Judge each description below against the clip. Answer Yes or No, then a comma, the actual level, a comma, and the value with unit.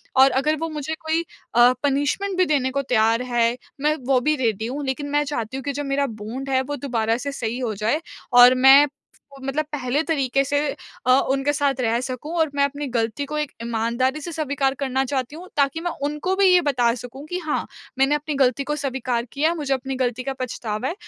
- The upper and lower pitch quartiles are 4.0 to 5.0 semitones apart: No, average, 2.8 semitones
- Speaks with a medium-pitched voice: No, very high, 275 Hz